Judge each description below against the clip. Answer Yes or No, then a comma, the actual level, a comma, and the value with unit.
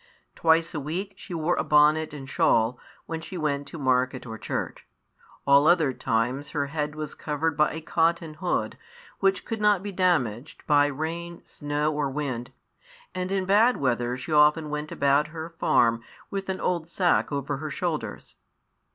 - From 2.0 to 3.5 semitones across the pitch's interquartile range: Yes, average, 3.2 semitones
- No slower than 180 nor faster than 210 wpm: No, average, 170 wpm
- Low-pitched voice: No, medium, 150 Hz